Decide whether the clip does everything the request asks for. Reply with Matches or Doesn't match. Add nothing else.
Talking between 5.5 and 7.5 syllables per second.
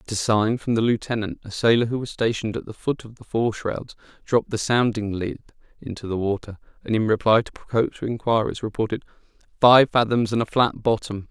Matches